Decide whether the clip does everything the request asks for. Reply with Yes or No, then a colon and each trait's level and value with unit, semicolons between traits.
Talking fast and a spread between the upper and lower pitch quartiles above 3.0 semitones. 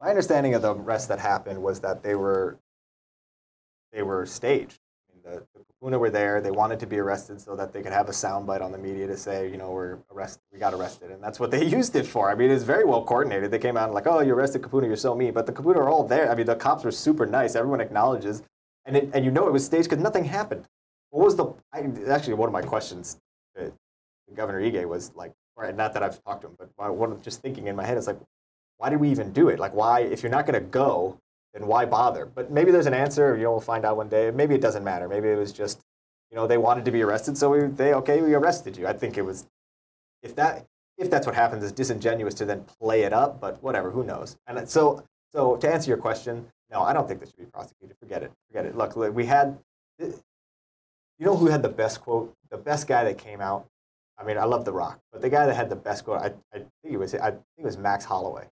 Yes: fast, 260 wpm; average, 5.1 semitones